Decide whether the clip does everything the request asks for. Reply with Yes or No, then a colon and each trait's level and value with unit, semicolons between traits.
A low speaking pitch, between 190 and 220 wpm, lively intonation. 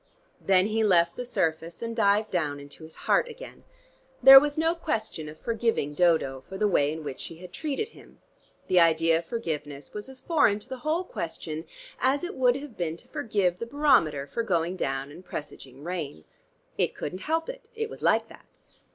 No: medium, 185 Hz; average, 195 wpm; wide, 8.5 semitones